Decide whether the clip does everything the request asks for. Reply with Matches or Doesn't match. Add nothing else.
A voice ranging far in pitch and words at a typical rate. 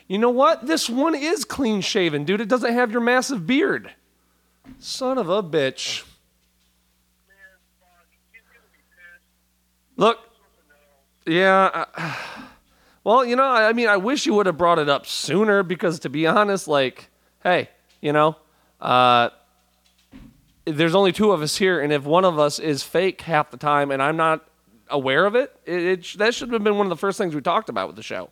Matches